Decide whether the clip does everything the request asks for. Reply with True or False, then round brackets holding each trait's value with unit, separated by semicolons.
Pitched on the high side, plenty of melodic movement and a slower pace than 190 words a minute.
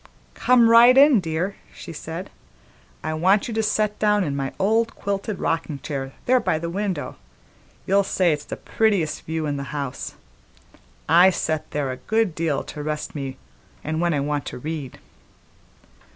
False (165 Hz; 5.8 semitones; 170 wpm)